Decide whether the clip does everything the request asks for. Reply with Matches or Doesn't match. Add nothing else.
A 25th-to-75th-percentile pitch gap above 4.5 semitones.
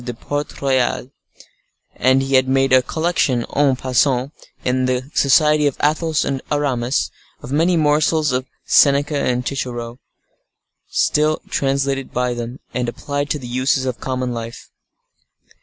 Doesn't match